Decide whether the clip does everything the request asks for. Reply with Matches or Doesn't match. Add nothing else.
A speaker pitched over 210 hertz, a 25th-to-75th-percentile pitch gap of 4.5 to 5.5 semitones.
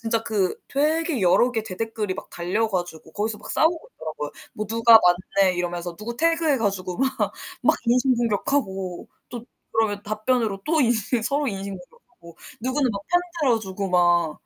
Matches